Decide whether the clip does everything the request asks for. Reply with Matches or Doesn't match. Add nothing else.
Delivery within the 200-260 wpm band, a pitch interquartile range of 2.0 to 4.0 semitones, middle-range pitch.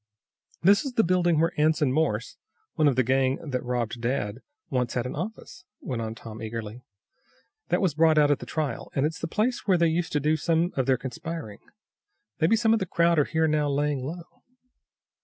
Doesn't match